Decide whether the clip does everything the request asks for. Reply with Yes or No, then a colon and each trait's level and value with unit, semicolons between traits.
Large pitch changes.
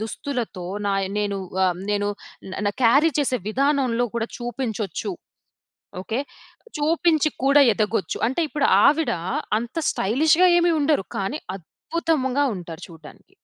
Yes: wide, 6.5 semitones